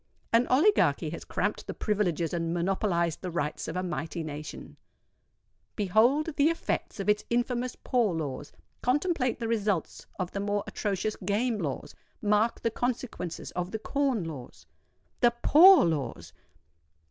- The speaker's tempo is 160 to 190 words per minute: No, slow, 135 wpm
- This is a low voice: No, high, 205 Hz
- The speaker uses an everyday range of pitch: No, wide, 6.2 semitones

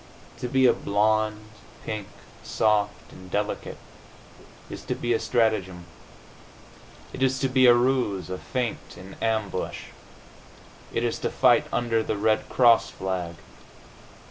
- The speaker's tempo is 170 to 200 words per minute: No, slow, 135 wpm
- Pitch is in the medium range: No, low, 110 Hz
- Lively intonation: No, average, 3.1 semitones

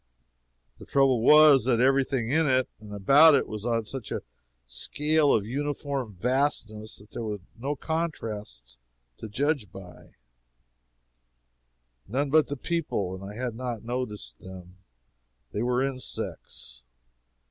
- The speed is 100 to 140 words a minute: Yes, slow, 135 wpm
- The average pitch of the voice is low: Yes, low, 125 Hz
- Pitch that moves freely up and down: No, average, 5.0 semitones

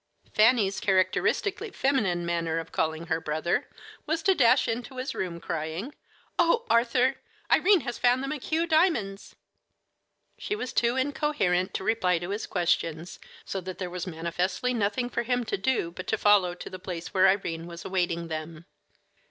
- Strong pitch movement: Yes, wide, 6.6 semitones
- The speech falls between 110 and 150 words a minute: No, average, 165 wpm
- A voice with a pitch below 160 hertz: No, high, 195 Hz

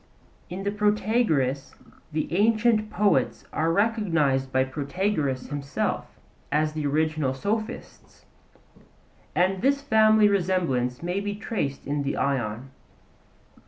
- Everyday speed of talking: No, slow, 110 wpm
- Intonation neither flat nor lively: No, wide, 7.0 semitones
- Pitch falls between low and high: Yes, medium, 170 Hz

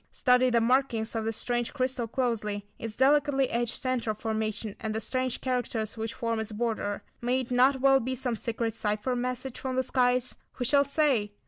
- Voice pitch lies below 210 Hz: No, high, 240 Hz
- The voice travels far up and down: No, narrow, 2.6 semitones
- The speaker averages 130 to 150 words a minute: No, average, 190 wpm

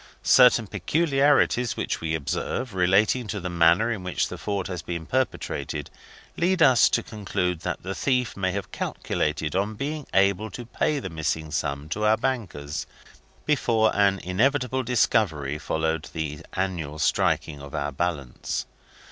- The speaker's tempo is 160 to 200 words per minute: No, average, 150 wpm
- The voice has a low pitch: Yes, very low, 95 Hz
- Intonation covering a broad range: Yes, wide, 6.9 semitones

